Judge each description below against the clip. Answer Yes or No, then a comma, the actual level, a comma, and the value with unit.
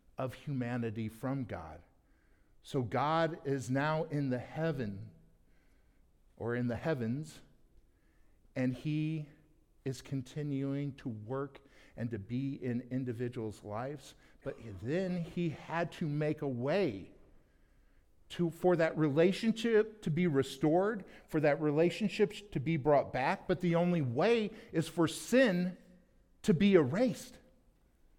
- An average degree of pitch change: No, wide, 5.8 semitones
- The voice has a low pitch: No, medium, 145 Hz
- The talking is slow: Yes, slow, 125 wpm